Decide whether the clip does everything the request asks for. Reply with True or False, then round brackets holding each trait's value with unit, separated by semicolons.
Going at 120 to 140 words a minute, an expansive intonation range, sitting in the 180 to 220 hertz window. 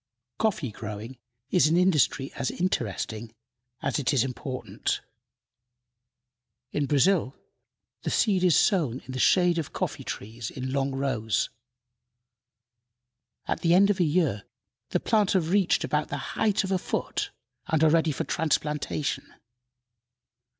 False (135 wpm; 5.8 semitones; 150 Hz)